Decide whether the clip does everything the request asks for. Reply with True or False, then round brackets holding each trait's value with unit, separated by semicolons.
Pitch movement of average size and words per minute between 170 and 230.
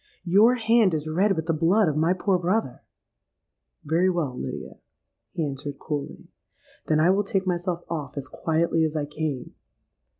False (3.6 semitones; 160 wpm)